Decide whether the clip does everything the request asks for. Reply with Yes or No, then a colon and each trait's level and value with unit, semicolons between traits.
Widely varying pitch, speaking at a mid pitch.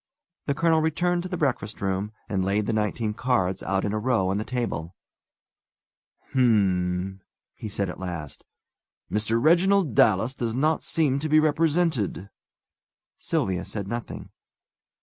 No: wide, 7.8 semitones; low, 110 Hz